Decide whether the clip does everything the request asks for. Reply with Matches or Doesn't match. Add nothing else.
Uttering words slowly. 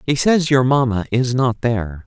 Doesn't match